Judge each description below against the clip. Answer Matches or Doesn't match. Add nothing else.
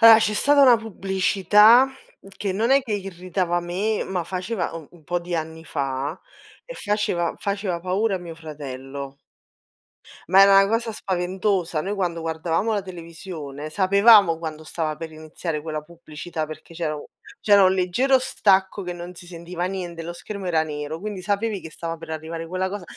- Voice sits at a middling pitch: Matches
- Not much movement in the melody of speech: Doesn't match